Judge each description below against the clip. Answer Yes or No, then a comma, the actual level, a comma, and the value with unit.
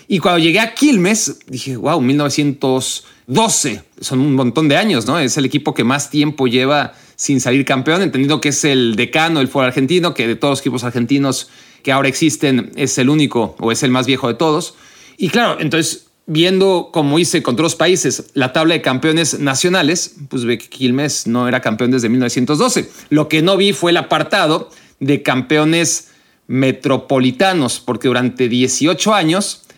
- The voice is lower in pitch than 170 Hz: Yes, medium, 140 Hz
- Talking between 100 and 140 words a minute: No, average, 180 wpm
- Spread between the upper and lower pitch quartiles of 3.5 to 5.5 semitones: Yes, average, 3.9 semitones